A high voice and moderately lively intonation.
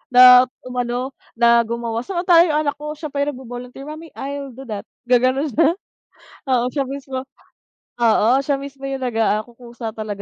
Yes: very high, 255 Hz; average, 3.0 semitones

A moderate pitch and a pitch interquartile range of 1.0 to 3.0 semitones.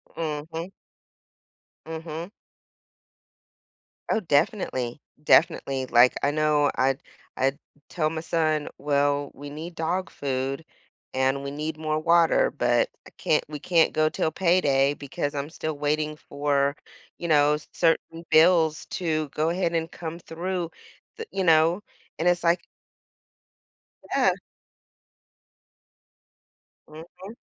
Yes: medium, 155 Hz; narrow, 2.6 semitones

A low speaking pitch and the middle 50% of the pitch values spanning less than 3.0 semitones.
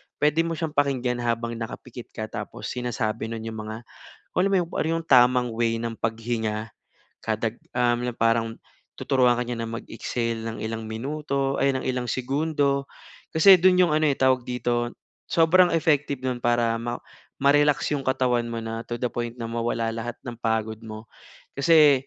No: low, 120 Hz; average, 3.3 semitones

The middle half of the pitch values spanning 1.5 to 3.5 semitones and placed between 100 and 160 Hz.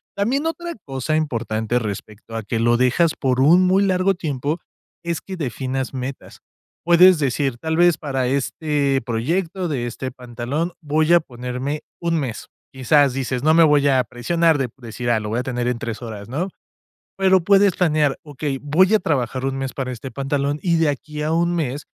No: average, 4.9 semitones; medium, 140 Hz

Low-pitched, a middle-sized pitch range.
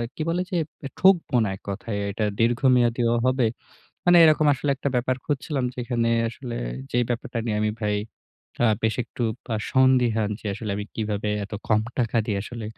Yes: low, 120 Hz; average, 3.1 semitones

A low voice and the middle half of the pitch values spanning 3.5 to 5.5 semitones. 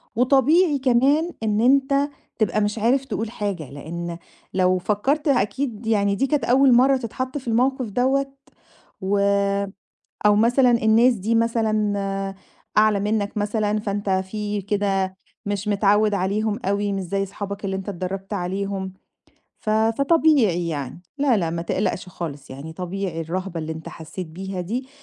No: high, 205 Hz; average, 4.2 semitones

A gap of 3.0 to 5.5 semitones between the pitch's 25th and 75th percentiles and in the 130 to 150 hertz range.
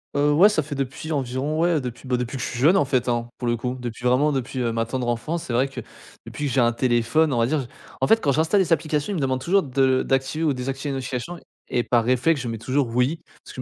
Yes: average, 3.5 semitones; low, 135 Hz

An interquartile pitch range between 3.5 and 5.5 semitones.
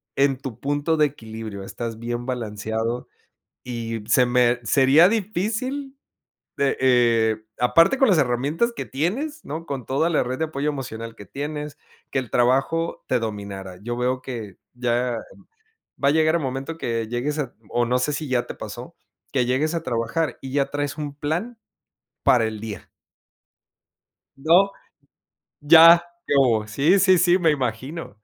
Yes: average, 5.0 semitones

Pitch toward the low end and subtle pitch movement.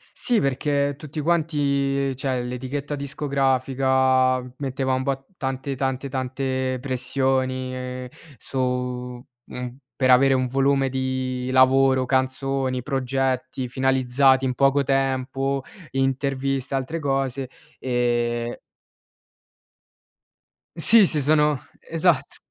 Yes: low, 130 Hz; narrow, 1.2 semitones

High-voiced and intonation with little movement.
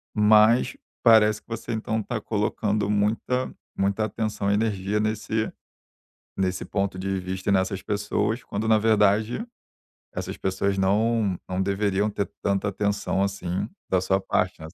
No: low, 105 Hz; narrow, 1.9 semitones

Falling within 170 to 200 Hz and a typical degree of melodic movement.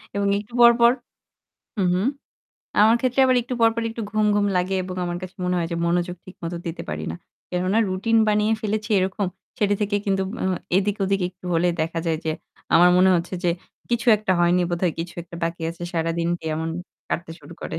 Yes: medium, 185 Hz; average, 3.6 semitones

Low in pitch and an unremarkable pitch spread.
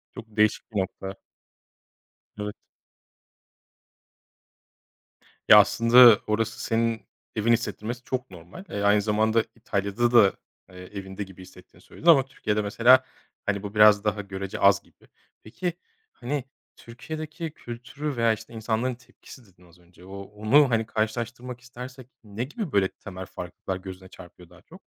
Yes: low, 110 Hz; average, 3.6 semitones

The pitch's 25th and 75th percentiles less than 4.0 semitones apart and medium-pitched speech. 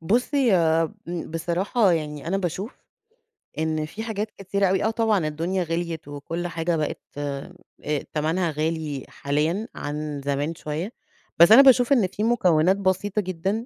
No: average, 4.6 semitones; medium, 175 Hz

